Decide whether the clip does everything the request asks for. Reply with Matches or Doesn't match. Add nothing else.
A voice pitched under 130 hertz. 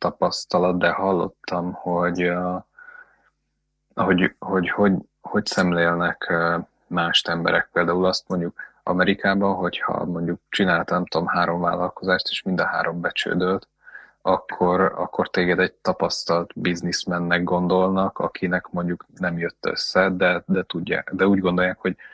Matches